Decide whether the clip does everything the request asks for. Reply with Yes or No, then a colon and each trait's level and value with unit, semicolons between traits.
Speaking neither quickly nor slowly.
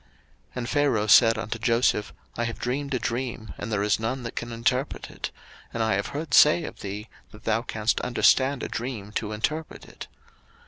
Yes: average, 195 wpm